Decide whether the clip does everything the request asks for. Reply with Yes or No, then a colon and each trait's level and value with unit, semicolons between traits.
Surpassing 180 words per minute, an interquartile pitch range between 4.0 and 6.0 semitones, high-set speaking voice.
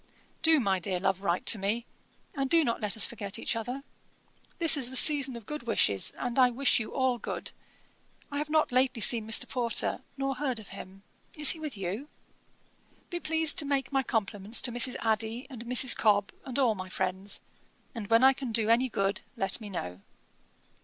Yes: average, 200 wpm; average, 4.7 semitones; high, 235 Hz